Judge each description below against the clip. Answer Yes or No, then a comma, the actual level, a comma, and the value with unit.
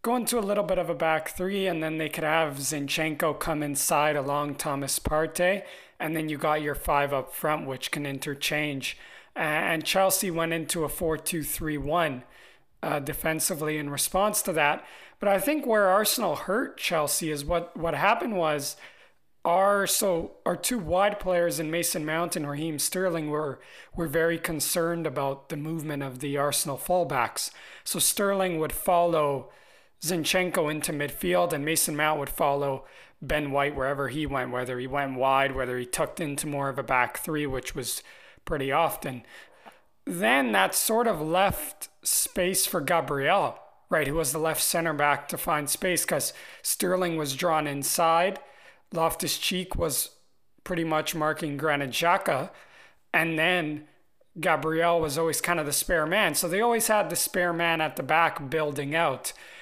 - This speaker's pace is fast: No, average, 165 wpm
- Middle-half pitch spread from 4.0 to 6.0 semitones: No, average, 3.1 semitones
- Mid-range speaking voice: Yes, medium, 160 Hz